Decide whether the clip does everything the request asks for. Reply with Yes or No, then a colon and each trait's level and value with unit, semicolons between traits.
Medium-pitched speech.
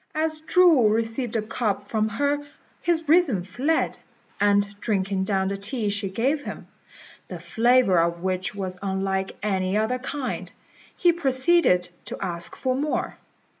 No: high, 215 Hz